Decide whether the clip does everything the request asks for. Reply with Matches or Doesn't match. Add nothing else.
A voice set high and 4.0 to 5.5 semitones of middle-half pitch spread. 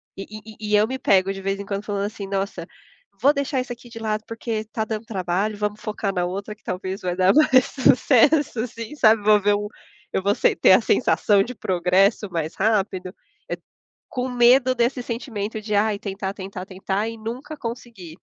Doesn't match